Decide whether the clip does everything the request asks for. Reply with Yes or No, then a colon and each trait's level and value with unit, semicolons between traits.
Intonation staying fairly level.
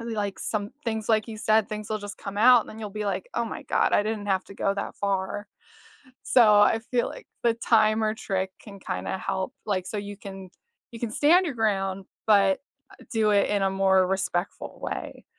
Yes: narrow, 2.2 semitones